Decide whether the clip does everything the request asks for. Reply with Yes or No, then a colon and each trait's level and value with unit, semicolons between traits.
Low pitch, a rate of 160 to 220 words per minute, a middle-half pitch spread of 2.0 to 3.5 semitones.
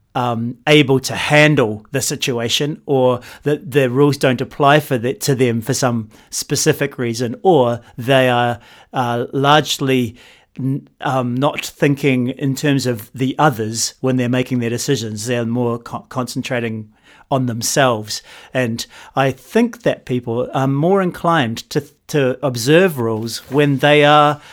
No: low, 130 Hz; average, 150 wpm; average, 3.1 semitones